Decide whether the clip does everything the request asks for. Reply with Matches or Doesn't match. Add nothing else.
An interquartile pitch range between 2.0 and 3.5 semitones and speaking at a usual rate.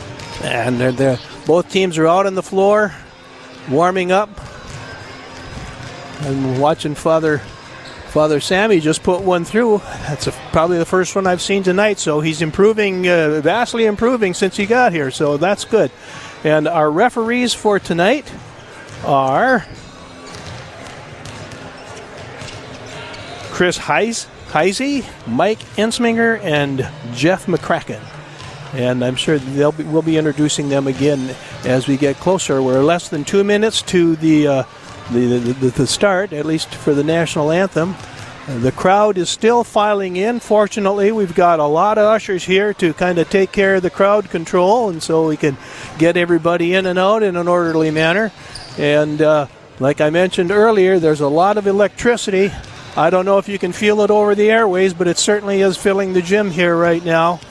Doesn't match